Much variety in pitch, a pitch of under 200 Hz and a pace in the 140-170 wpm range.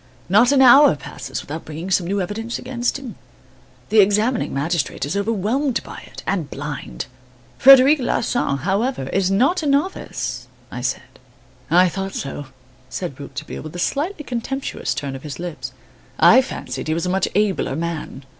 Yes: wide, 8.8 semitones; high, 190 Hz; average, 165 wpm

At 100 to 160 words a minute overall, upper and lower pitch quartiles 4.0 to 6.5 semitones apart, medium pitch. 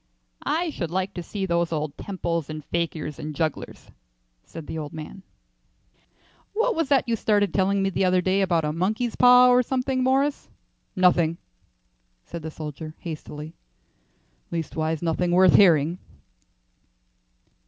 Yes: average, 145 wpm; average, 4.3 semitones; medium, 175 Hz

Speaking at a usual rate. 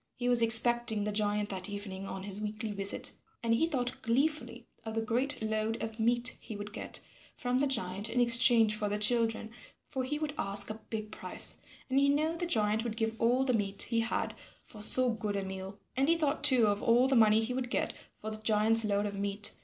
No: fast, 225 wpm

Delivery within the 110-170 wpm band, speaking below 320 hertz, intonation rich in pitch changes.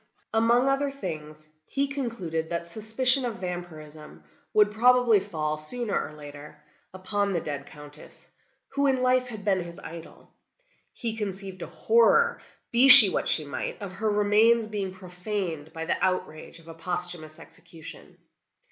Yes: average, 150 wpm; high, 190 Hz; wide, 6.1 semitones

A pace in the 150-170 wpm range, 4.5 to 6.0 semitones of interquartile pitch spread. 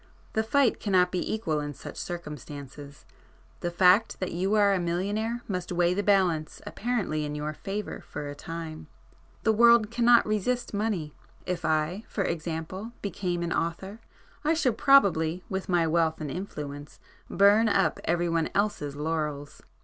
Yes: average, 155 wpm; average, 4.8 semitones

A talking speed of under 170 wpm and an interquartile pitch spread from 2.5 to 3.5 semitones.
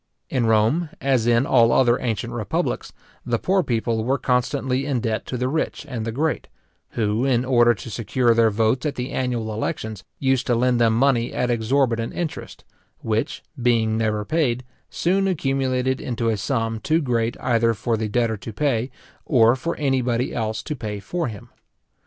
No: average, 180 wpm; average, 2.8 semitones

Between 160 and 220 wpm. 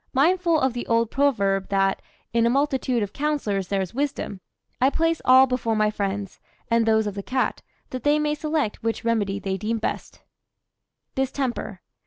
Yes: average, 175 wpm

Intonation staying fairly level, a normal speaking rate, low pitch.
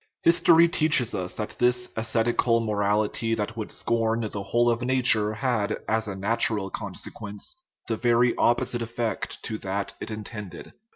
Yes: narrow, 2.2 semitones; average, 155 wpm; low, 115 Hz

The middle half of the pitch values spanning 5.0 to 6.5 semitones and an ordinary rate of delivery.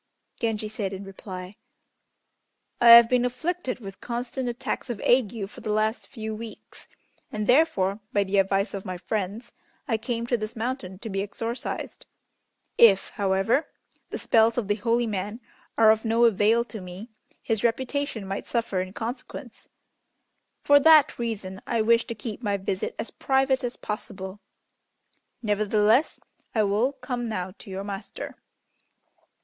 No: average, 3.2 semitones; average, 155 wpm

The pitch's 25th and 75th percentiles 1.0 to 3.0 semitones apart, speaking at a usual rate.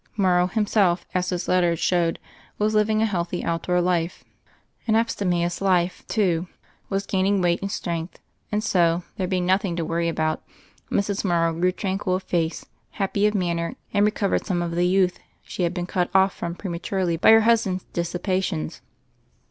Yes: narrow, 2.4 semitones; average, 175 wpm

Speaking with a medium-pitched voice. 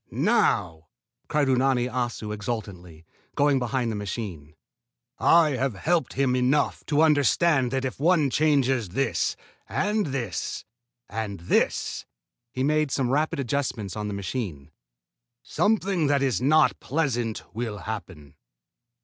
No: low, 130 Hz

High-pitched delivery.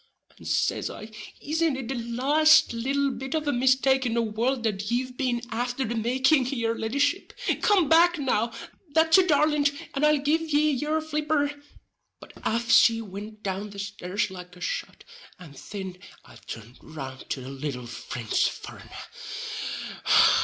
Yes: high, 245 Hz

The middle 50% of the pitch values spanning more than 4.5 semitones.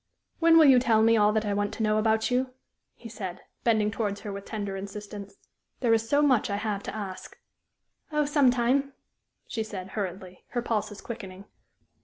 No: average, 3.1 semitones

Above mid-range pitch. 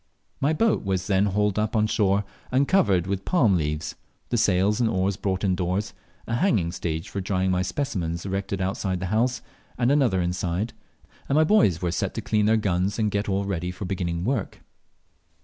No: low, 100 Hz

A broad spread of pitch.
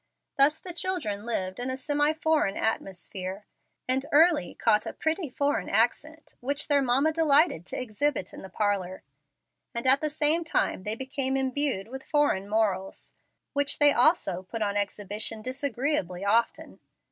Yes: wide, 6.3 semitones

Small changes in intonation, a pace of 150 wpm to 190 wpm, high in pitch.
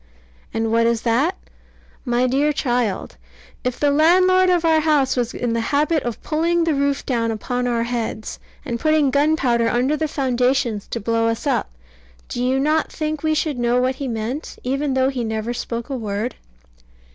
No: average, 4.3 semitones; average, 180 wpm; very high, 255 Hz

